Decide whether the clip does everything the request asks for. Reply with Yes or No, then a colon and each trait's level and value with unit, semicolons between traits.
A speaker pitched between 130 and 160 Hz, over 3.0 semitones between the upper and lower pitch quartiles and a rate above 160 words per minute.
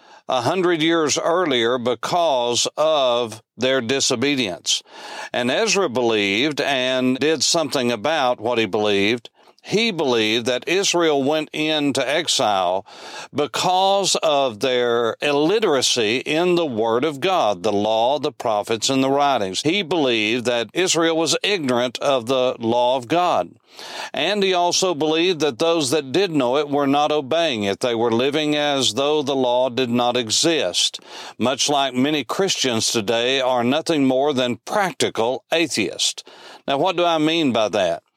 No: medium, 140 Hz; average, 4.7 semitones; average, 150 wpm